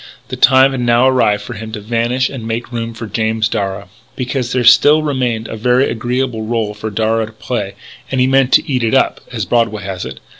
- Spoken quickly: Yes, fast, 220 wpm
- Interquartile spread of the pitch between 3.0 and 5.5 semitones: No, narrow, 2.5 semitones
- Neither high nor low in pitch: No, low, 115 Hz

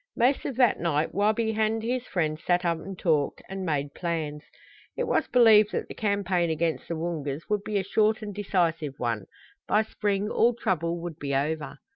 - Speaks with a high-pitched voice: No, medium, 180 Hz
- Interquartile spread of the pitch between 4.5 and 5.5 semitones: Yes, average, 5.1 semitones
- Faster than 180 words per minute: Yes, average, 190 wpm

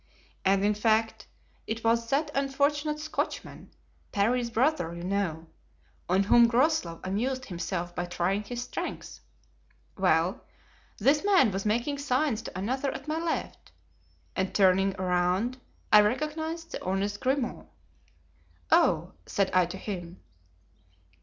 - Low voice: No, high, 220 Hz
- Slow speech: Yes, slow, 125 wpm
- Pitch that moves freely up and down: Yes, wide, 6.2 semitones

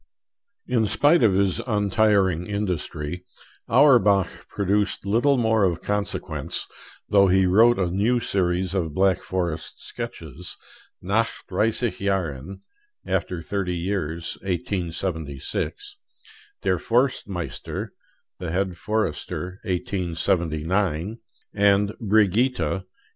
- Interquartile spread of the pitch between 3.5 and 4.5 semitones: No, average, 3.1 semitones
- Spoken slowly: Yes, slow, 100 wpm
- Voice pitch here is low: Yes, very low, 95 Hz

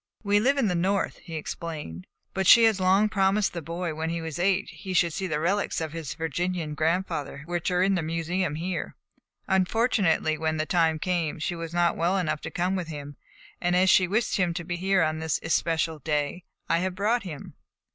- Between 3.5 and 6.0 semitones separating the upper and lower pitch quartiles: No, average, 2.9 semitones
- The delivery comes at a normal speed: No, fast, 215 wpm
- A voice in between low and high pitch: Yes, medium, 175 Hz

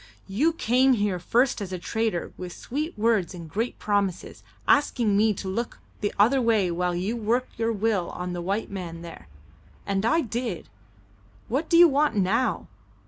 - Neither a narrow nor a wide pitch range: Yes, average, 4.6 semitones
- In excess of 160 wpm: Yes, average, 175 wpm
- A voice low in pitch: No, high, 215 Hz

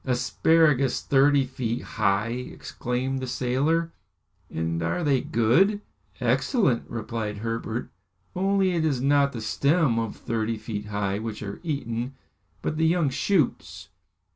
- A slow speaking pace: Yes, slow, 130 wpm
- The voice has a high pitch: No, low, 130 Hz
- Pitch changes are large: No, average, 4.8 semitones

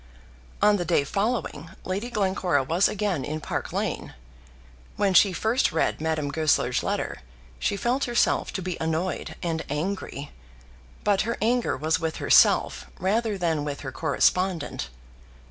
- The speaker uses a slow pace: No, average, 145 wpm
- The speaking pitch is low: No, medium, 180 Hz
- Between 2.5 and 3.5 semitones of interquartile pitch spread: No, average, 4.8 semitones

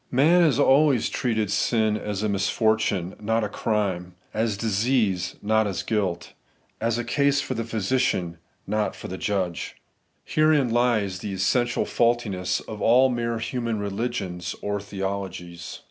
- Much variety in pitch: No, average, 3.6 semitones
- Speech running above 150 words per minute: No, average, 145 wpm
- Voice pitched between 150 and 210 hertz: No, low, 110 Hz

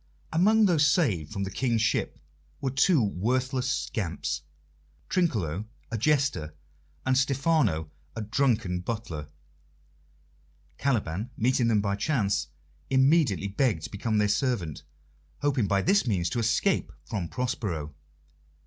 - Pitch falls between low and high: No, low, 115 Hz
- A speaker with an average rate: No, slow, 120 wpm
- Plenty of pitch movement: Yes, wide, 5.7 semitones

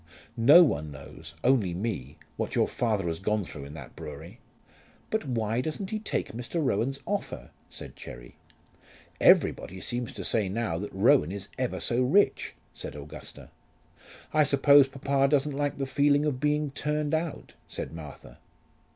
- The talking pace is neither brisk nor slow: Yes, average, 160 wpm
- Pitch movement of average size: No, wide, 7.7 semitones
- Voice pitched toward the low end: Yes, low, 120 Hz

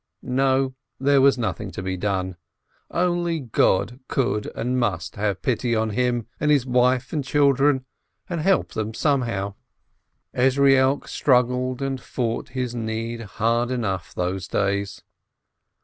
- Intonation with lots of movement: No, average, 3.9 semitones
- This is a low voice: Yes, low, 125 Hz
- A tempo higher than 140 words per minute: No, slow, 135 wpm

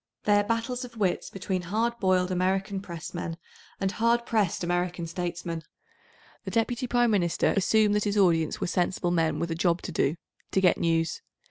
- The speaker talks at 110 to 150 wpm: No, average, 165 wpm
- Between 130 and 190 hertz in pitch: Yes, medium, 185 Hz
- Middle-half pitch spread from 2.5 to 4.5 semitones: Yes, average, 3.7 semitones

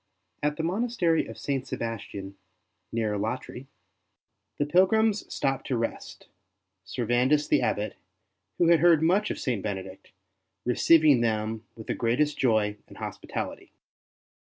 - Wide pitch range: Yes, wide, 6.5 semitones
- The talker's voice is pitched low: Yes, low, 130 Hz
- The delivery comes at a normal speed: No, slow, 130 wpm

